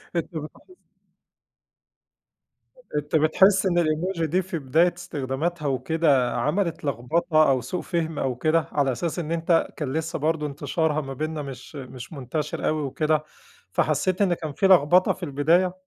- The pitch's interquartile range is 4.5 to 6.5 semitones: No, average, 3.1 semitones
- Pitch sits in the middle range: Yes, medium, 155 Hz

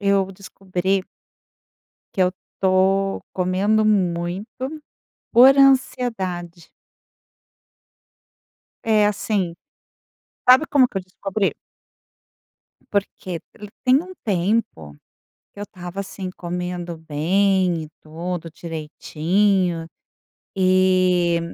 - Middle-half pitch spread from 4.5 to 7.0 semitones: No, average, 2.8 semitones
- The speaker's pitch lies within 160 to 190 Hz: Yes, medium, 185 Hz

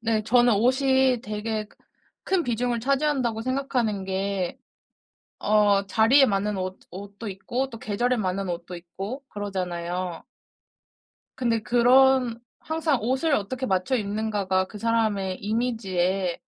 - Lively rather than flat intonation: No, average, 4.3 semitones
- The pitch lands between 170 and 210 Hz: No, high, 220 Hz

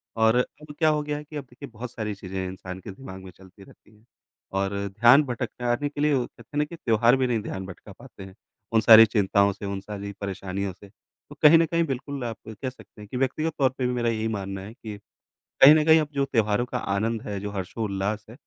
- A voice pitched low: Yes, low, 115 Hz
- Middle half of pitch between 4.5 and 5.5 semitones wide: Yes, average, 5.2 semitones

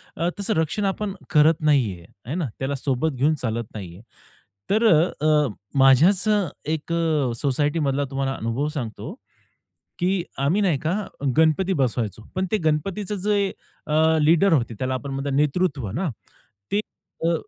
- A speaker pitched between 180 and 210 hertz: No, medium, 150 Hz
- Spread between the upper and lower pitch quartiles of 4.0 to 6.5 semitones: Yes, average, 4.5 semitones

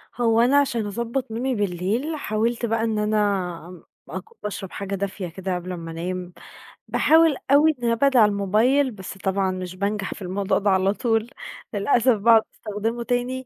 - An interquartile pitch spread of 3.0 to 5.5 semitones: Yes, average, 3.9 semitones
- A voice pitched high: Yes, high, 210 Hz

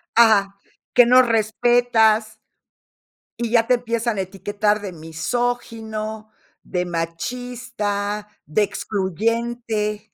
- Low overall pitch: No, high, 220 Hz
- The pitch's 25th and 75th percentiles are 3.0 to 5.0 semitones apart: No, narrow, 2.6 semitones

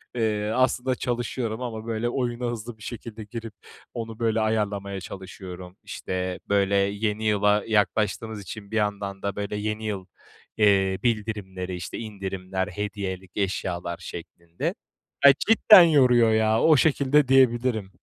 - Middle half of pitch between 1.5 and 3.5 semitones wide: Yes, average, 2.9 semitones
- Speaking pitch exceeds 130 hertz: No, low, 105 Hz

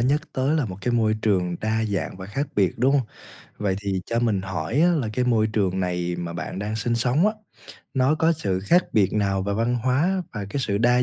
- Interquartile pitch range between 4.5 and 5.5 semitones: Yes, average, 5.1 semitones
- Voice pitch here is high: No, low, 110 Hz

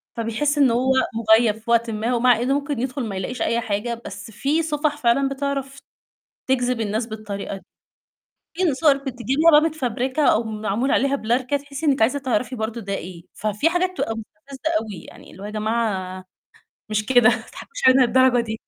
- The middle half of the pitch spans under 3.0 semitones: No, average, 4.0 semitones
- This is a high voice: Yes, high, 245 Hz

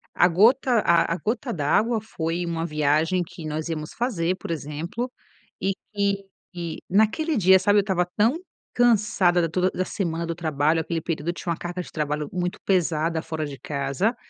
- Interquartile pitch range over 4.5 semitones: No, average, 3.9 semitones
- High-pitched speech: No, medium, 175 Hz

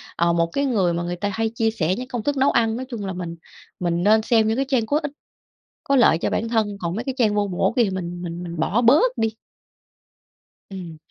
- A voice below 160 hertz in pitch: No, high, 215 Hz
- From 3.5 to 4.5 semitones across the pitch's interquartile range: No, wide, 5.4 semitones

